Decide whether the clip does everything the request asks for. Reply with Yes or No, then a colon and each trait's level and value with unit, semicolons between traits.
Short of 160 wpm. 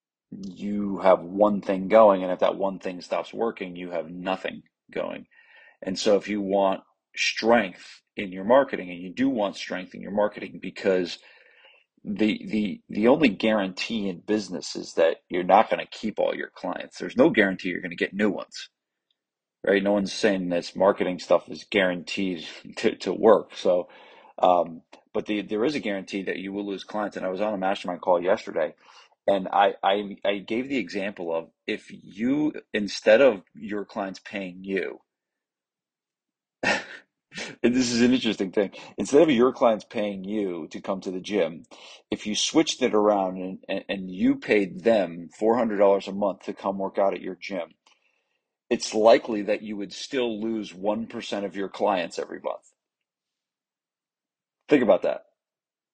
No: average, 180 wpm